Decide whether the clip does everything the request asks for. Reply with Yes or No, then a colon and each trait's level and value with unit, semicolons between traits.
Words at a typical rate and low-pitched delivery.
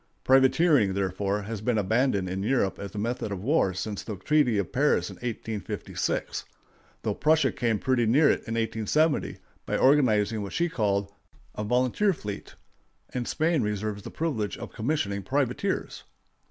Yes: average, 155 wpm; low, 115 Hz